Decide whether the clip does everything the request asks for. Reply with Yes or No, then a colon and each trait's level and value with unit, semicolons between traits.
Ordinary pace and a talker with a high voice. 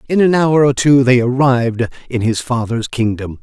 No: average, 195 wpm; low, 125 Hz